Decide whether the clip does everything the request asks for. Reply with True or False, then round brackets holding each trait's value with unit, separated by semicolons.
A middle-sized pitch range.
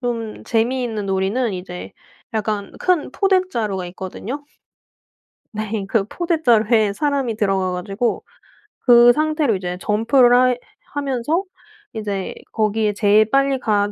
True (4.0 semitones)